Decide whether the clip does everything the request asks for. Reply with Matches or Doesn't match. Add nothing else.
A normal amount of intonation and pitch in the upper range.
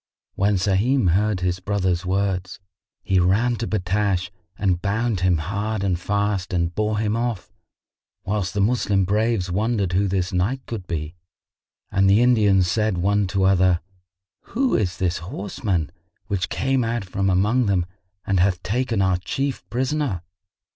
Doesn't match